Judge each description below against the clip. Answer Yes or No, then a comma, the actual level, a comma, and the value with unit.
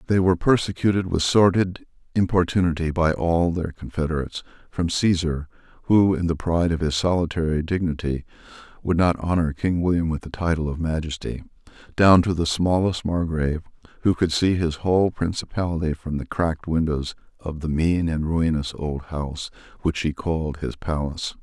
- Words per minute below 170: Yes, average, 160 wpm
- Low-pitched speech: Yes, very low, 85 Hz